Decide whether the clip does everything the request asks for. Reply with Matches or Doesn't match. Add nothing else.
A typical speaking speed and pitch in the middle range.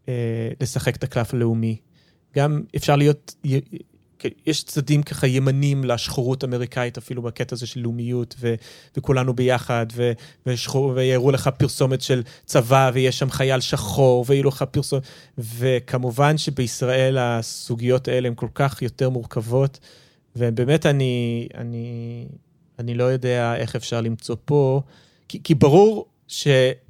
Doesn't match